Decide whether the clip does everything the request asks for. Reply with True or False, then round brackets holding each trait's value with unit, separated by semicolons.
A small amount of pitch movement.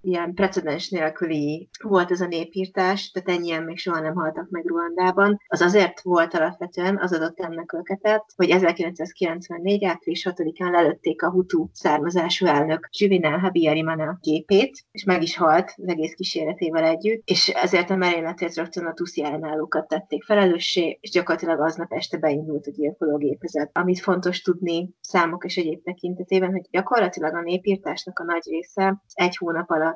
True (2.2 semitones)